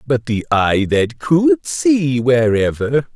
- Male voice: Yes, male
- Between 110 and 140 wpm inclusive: Yes, slow, 135 wpm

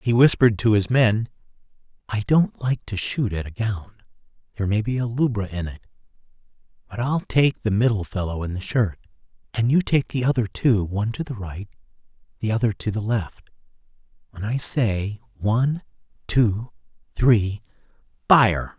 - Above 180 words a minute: No, average, 165 wpm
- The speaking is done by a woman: No, male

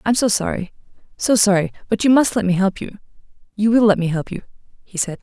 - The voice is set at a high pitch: Yes, high, 200 Hz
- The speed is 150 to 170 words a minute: No, fast, 205 wpm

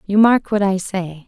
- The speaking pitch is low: No, high, 195 Hz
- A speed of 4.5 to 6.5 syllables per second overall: No, 4.3 syllables/s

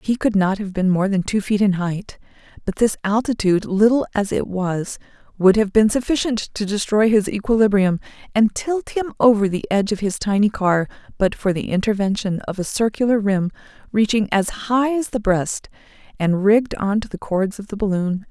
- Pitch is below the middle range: No, high, 205 Hz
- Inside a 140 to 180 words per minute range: No, average, 195 wpm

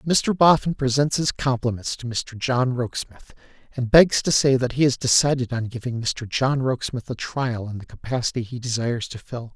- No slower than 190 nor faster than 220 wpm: Yes, average, 195 wpm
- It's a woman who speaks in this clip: No, male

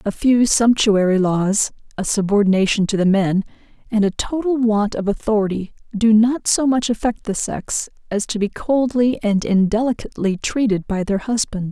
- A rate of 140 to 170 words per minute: Yes, average, 165 wpm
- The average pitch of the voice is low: No, high, 215 Hz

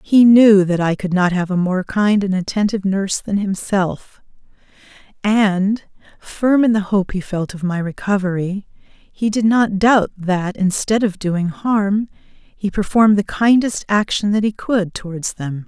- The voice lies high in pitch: Yes, high, 200 Hz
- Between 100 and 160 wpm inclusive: No, average, 170 wpm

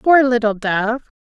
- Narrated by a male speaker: No, female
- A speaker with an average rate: Yes, average, 145 wpm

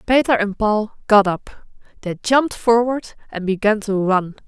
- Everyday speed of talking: Yes, average, 160 wpm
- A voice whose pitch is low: No, high, 215 Hz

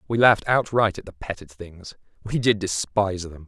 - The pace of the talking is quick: No, average, 190 wpm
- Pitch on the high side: No, low, 100 Hz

